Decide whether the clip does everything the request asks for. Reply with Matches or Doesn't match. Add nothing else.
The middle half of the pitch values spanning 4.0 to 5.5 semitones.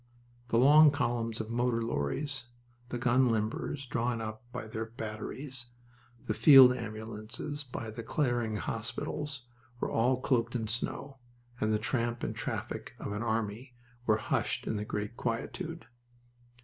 Doesn't match